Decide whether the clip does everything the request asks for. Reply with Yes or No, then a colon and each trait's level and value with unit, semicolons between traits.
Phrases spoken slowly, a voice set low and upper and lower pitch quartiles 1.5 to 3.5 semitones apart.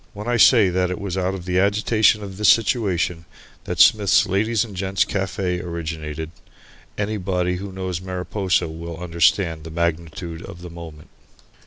No: average, 160 wpm; very low, 90 Hz; average, 2.9 semitones